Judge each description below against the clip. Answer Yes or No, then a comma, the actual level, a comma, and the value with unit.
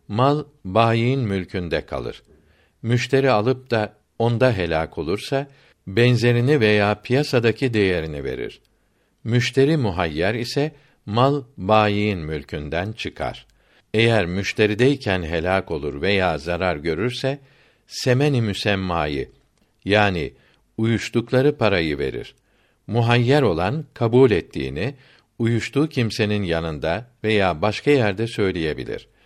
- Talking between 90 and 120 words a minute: Yes, slow, 95 wpm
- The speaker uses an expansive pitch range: No, average, 4.8 semitones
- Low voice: Yes, low, 110 Hz